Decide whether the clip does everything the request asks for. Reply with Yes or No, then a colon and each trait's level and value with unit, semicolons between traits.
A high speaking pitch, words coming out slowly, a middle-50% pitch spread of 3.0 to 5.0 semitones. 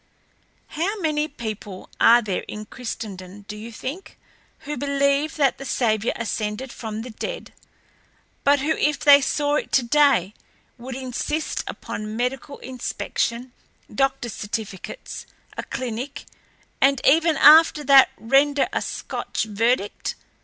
Yes: very high, 260 Hz; slow, 125 wpm; average, 4.7 semitones